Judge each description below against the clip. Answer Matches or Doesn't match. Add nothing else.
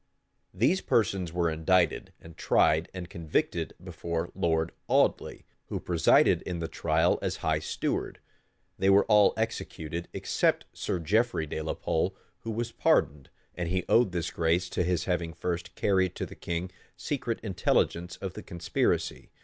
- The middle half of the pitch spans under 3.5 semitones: Matches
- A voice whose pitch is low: Matches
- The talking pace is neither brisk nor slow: Matches